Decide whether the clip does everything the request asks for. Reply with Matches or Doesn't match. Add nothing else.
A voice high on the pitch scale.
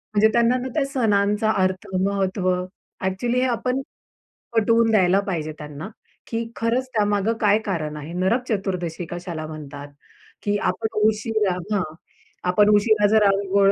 Matches